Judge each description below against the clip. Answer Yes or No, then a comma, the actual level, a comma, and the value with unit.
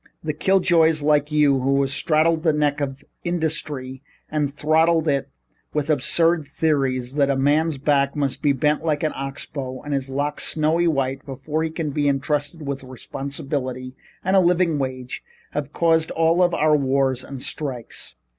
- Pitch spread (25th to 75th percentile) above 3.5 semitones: No, narrow, 2.6 semitones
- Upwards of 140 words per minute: Yes, average, 170 wpm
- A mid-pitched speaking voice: Yes, medium, 145 Hz